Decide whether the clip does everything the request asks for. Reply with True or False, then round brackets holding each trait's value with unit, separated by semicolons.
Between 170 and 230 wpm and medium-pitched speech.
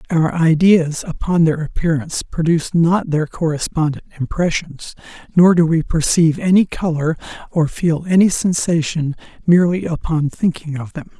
False (135 wpm; 160 Hz)